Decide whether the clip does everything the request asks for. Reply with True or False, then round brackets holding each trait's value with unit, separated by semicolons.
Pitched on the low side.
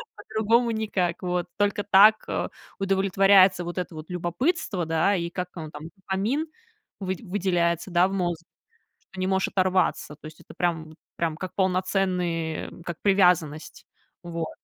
False (185 Hz)